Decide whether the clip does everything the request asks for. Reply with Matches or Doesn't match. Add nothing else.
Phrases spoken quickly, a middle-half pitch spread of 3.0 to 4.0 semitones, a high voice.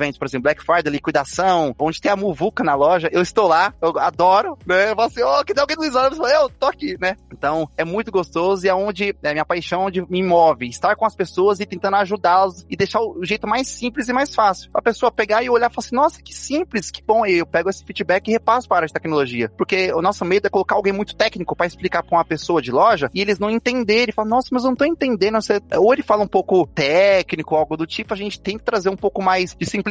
Doesn't match